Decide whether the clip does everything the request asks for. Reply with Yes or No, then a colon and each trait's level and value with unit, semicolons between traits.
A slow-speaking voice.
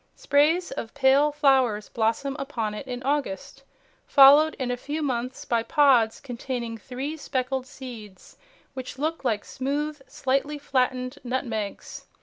Yes: slow, 130 wpm